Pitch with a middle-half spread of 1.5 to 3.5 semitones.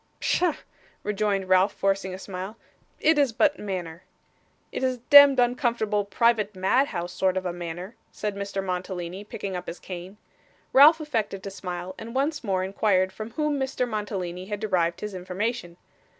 No: average, 4.1 semitones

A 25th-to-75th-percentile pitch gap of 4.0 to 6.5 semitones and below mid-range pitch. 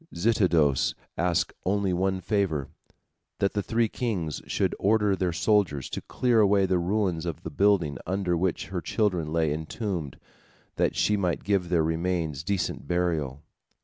No: average, 3.6 semitones; very low, 90 Hz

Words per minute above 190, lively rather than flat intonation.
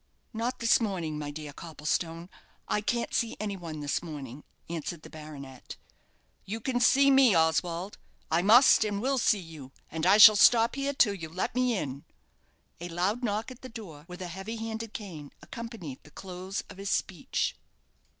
No: average, 180 wpm; wide, 6.0 semitones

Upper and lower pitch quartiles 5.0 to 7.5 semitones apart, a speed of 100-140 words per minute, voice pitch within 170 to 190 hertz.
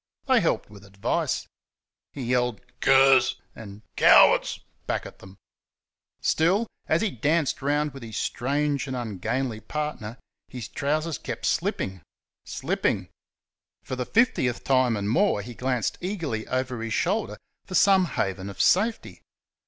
No: wide, 5.4 semitones; slow, 135 wpm; low, 130 Hz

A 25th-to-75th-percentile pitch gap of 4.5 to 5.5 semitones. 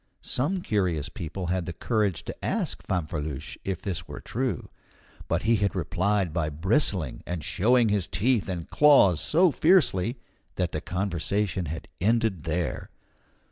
Yes: average, 4.9 semitones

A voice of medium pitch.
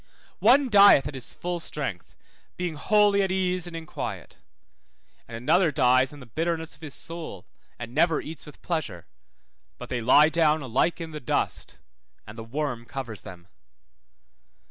Yes: medium, 155 Hz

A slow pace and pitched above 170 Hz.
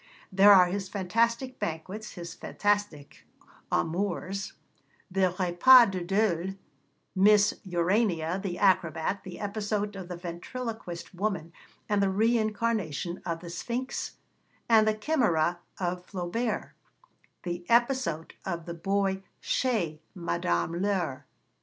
Yes: slow, 115 wpm; high, 190 Hz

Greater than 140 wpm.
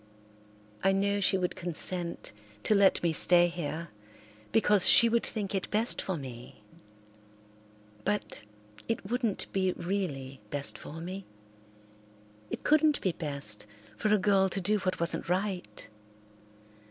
No: slow, 135 wpm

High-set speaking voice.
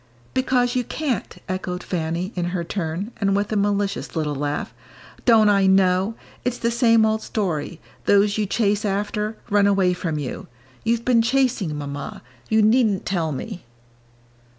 Yes: high, 200 Hz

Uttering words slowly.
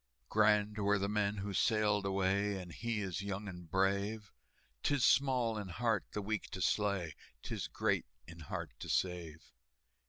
No: average, 160 wpm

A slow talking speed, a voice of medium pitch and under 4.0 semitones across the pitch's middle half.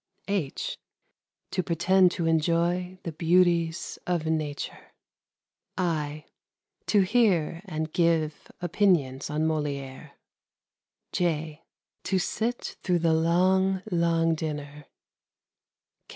Yes: slow, 95 wpm; medium, 165 Hz; average, 2.7 semitones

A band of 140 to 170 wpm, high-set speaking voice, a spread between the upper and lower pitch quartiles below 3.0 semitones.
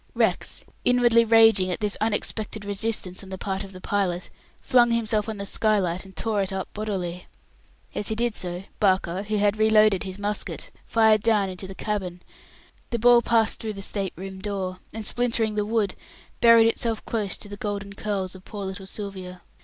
No: average, 185 wpm; high, 205 Hz; narrow, 2.5 semitones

